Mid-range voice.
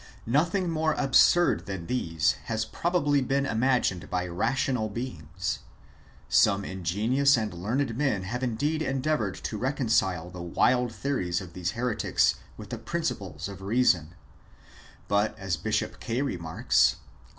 No: low, 110 Hz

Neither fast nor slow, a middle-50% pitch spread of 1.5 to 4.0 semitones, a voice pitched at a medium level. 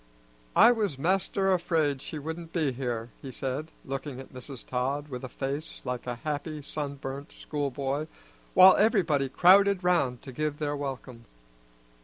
Yes: average, 150 wpm; average, 3.6 semitones; medium, 145 Hz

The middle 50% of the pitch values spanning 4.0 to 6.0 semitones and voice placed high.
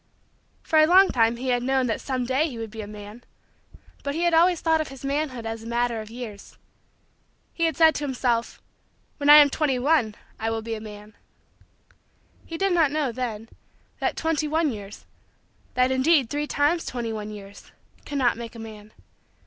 Yes: average, 5.1 semitones; very high, 255 Hz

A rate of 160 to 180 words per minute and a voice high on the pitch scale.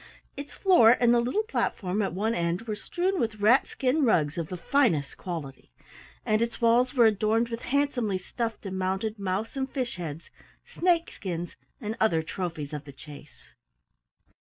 Yes: average, 170 wpm; high, 215 Hz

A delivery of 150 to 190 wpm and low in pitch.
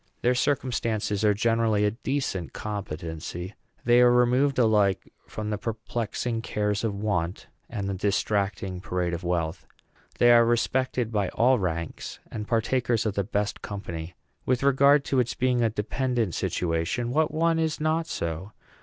Yes: average, 155 wpm; low, 110 Hz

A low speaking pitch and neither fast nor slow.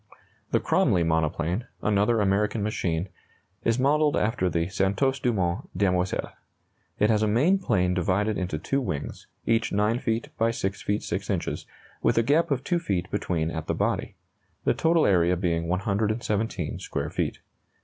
Yes: low, 105 Hz; average, 160 wpm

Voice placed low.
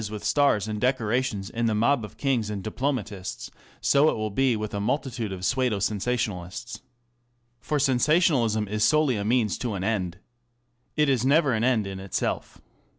Yes: low, 115 Hz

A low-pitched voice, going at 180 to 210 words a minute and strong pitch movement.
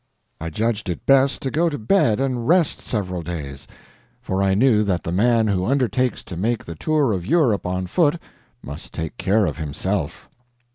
Yes: low, 105 Hz; average, 185 wpm; wide, 6.5 semitones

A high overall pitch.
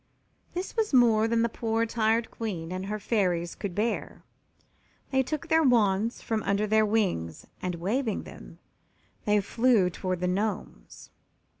Yes: high, 215 Hz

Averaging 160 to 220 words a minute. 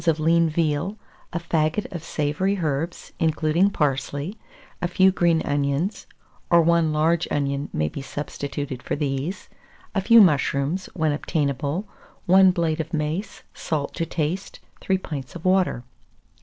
No: average, 140 wpm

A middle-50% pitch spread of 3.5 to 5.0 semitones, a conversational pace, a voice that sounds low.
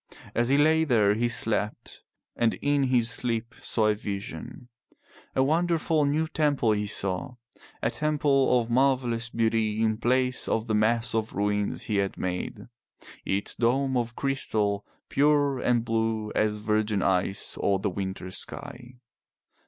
Yes: average, 3.9 semitones; average, 145 wpm; low, 115 Hz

